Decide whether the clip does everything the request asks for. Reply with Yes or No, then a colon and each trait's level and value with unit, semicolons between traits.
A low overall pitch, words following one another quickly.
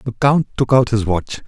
Yes: low, 120 Hz; fast, 245 wpm